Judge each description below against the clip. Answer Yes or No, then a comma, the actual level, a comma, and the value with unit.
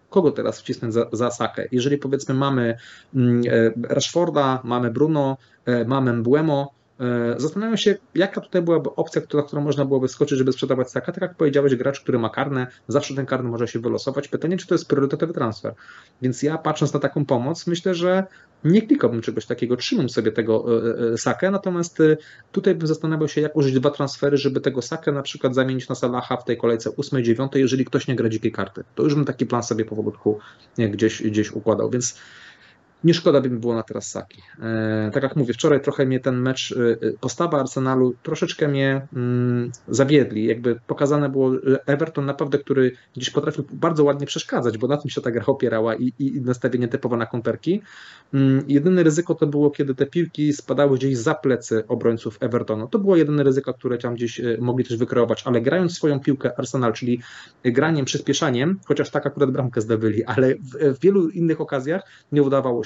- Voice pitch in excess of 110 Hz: Yes, low, 135 Hz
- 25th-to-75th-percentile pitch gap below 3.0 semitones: No, average, 3.4 semitones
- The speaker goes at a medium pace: No, fast, 180 wpm